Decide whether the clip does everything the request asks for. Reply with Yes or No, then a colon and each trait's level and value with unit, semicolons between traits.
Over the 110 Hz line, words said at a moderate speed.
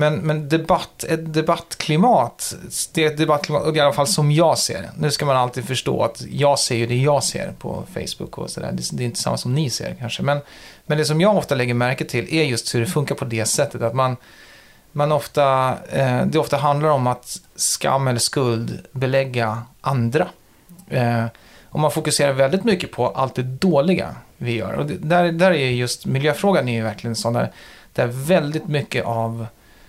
No: medium, 140 Hz; fast, 200 wpm